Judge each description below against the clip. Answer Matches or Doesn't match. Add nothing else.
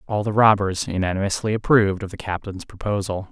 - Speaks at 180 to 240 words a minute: Doesn't match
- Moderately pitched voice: Doesn't match